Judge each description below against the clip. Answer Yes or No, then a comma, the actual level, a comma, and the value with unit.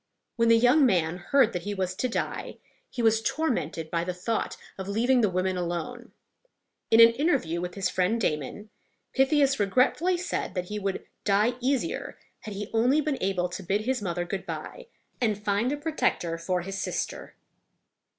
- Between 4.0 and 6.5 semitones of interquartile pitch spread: Yes, wide, 5.5 semitones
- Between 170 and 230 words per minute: Yes, average, 180 wpm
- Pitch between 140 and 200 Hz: No, high, 210 Hz